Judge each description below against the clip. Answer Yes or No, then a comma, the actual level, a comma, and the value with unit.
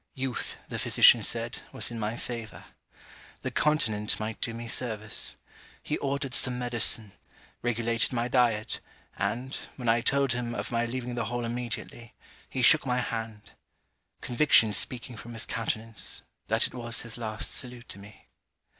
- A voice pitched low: Yes, low, 120 Hz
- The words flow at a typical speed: Yes, average, 155 wpm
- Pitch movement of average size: No, narrow, 1.7 semitones